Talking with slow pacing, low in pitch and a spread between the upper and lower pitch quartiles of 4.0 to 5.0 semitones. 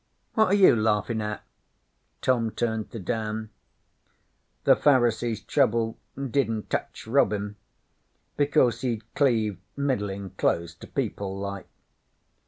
No: slow, 110 wpm; low, 110 Hz; average, 3.2 semitones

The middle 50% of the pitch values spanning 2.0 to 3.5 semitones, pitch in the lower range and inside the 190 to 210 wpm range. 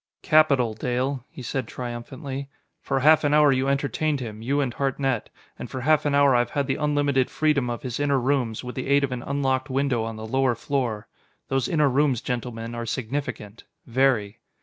Yes: average, 2.8 semitones; low, 130 Hz; average, 195 wpm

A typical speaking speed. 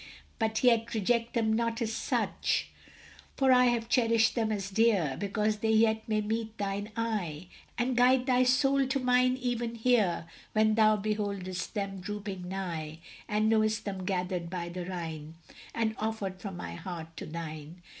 Yes: average, 165 wpm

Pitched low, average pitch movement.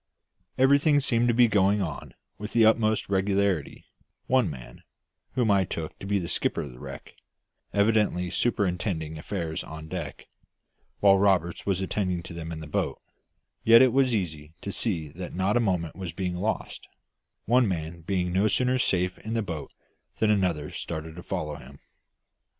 Yes: very low, 95 Hz; average, 4.5 semitones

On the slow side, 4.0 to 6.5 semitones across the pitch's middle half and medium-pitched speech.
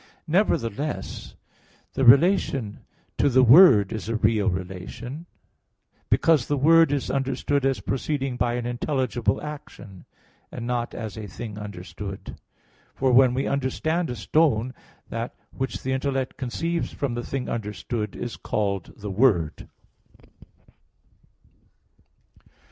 No: slow, 120 wpm; average, 4.3 semitones; low, 125 Hz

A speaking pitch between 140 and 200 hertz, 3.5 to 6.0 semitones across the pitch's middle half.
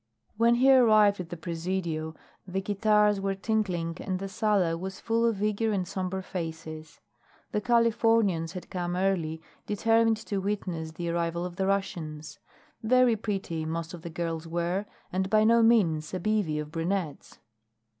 Yes: high, 190 Hz; average, 4.2 semitones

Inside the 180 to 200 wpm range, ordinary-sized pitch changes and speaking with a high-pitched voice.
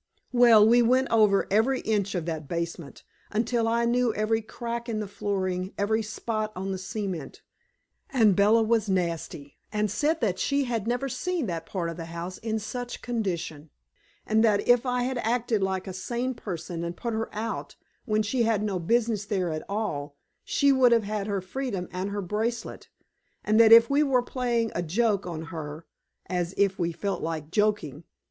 Yes: average, 185 wpm; average, 4.3 semitones; high, 215 Hz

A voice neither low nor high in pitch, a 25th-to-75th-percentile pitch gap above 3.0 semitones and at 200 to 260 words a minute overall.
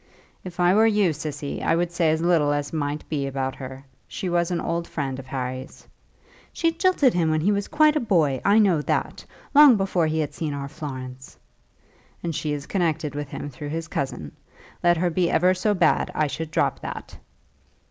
Yes: medium, 160 Hz; average, 4.0 semitones; fast, 205 wpm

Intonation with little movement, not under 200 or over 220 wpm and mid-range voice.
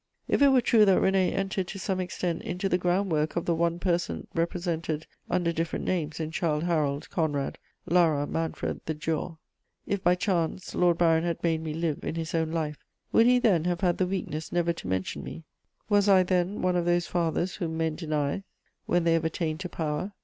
Yes: narrow, 2.2 semitones; fast, 205 wpm; medium, 170 Hz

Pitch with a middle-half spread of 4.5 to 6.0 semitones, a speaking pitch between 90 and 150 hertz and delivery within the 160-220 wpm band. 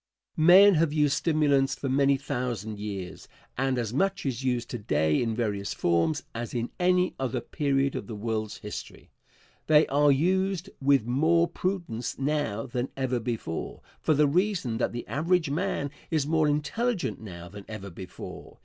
Yes: wide, 5.5 semitones; low, 135 Hz; average, 165 wpm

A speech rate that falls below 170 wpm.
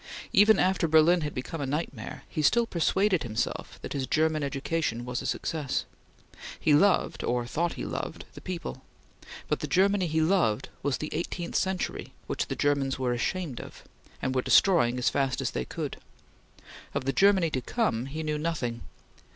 No: average, 175 wpm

